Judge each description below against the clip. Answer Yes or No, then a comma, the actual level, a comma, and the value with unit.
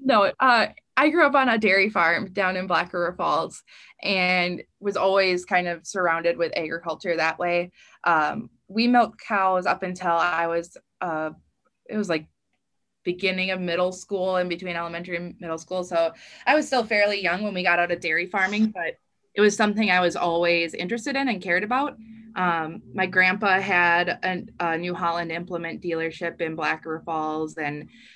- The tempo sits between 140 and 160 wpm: No, average, 185 wpm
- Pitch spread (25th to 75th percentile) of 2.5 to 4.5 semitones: Yes, average, 2.9 semitones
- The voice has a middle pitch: Yes, medium, 180 Hz